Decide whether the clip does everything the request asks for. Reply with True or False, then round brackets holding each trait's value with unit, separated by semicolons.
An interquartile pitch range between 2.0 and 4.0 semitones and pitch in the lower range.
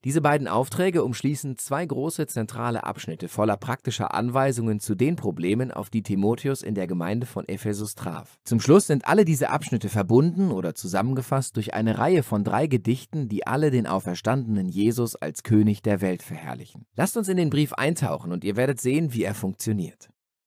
False (5.0 semitones; 120 Hz)